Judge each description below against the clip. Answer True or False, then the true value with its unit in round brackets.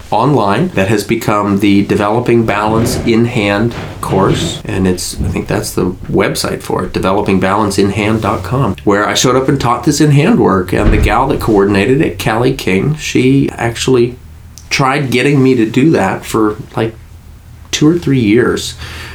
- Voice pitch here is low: True (105 Hz)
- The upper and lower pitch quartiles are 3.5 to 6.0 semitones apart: True (4.2 semitones)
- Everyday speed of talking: True (165 wpm)